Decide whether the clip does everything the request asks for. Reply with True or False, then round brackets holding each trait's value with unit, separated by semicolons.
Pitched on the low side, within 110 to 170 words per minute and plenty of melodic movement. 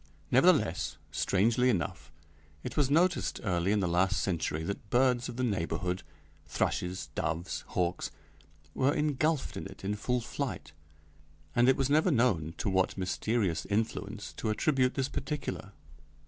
True (110 Hz; 145 wpm; 5.9 semitones)